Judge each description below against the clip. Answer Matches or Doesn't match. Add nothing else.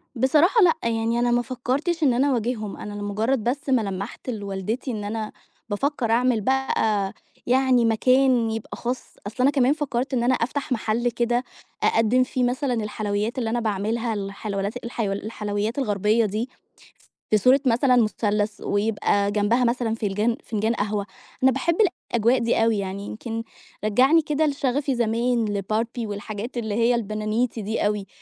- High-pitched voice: Matches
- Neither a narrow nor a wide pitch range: Matches